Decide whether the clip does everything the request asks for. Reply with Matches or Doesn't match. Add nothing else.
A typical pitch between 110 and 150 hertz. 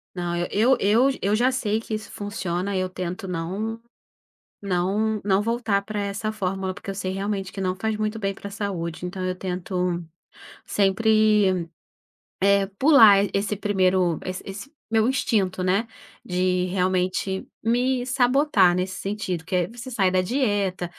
Doesn't match